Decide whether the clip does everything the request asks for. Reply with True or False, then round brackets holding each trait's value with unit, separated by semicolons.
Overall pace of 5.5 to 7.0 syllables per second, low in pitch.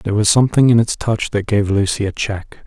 True (5.7 syllables/s; 105 Hz)